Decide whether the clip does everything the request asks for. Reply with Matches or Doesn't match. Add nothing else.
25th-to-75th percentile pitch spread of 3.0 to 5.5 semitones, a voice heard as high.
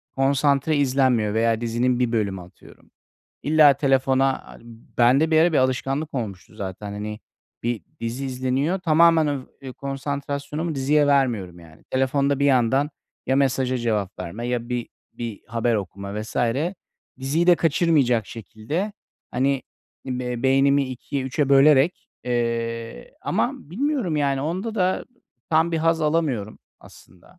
Doesn't match